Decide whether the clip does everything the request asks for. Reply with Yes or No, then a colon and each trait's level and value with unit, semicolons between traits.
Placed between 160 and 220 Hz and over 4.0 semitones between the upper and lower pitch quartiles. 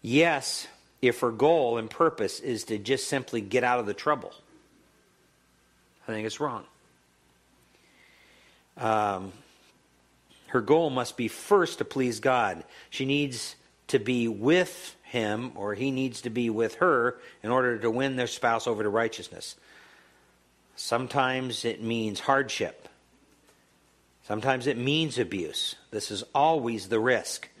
No: low, 115 Hz; average, 4.4 semitones